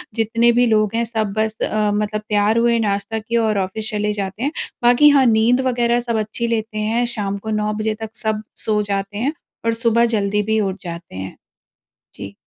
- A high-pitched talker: Yes, high, 220 Hz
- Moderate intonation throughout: No, narrow, 1.9 semitones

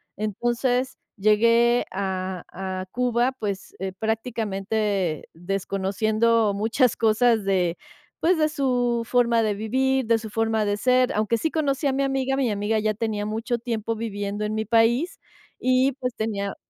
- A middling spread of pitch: Yes, average, 3.2 semitones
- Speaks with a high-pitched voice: Yes, high, 225 Hz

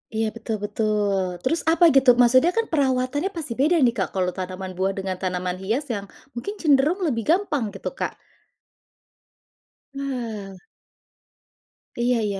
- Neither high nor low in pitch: No, high, 230 Hz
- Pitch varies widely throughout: Yes, wide, 6.1 semitones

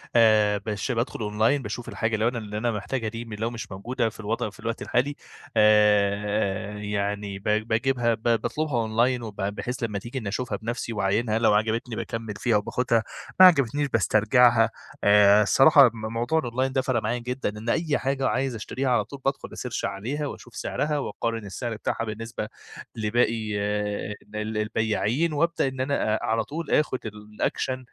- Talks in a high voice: No, low, 115 Hz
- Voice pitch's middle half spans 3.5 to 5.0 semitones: No, average, 3.0 semitones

